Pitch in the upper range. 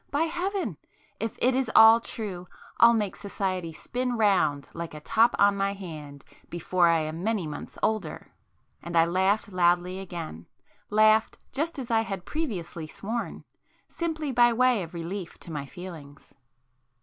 Yes: high, 195 Hz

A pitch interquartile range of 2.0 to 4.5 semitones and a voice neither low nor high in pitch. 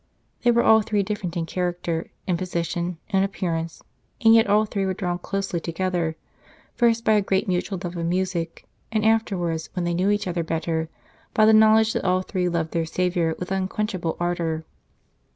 Yes: average, 3.3 semitones; medium, 180 Hz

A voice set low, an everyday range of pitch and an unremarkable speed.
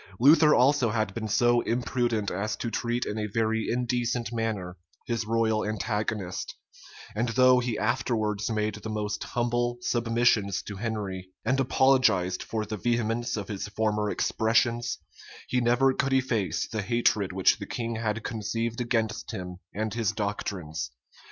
No: low, 115 Hz; narrow, 2.2 semitones; average, 150 wpm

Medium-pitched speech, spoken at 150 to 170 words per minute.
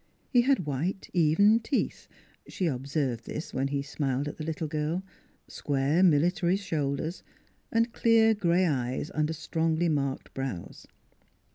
No: medium, 155 Hz; slow, 135 wpm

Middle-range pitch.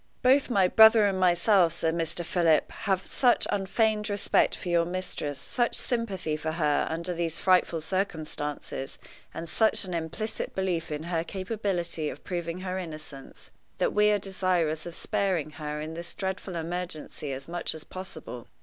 Yes: medium, 175 Hz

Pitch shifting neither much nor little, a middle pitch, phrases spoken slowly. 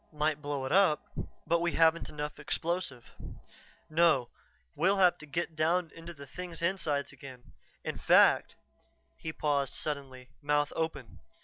No: average, 3.0 semitones; medium, 155 Hz; average, 145 wpm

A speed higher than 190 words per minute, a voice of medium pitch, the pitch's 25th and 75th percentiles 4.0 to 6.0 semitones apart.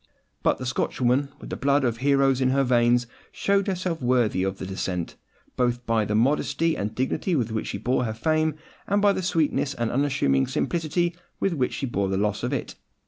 No: fast, 205 wpm; low, 130 Hz; average, 5.3 semitones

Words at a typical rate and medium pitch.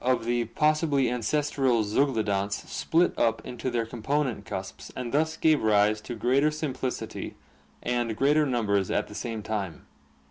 No: average, 145 wpm; low, 120 Hz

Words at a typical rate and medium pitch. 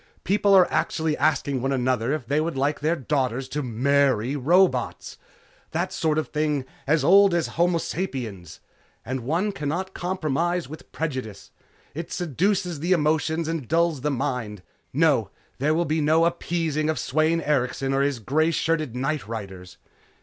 Yes: average, 155 wpm; medium, 150 Hz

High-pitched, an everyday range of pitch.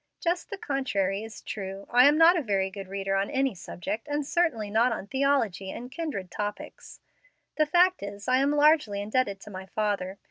No: high, 220 Hz; wide, 6.5 semitones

